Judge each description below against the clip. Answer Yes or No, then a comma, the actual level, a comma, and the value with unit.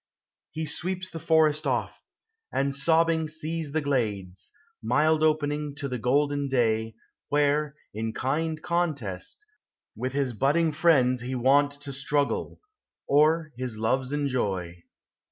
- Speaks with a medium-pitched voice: Yes, medium, 145 Hz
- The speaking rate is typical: No, slow, 125 wpm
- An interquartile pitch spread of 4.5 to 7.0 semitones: No, average, 3.6 semitones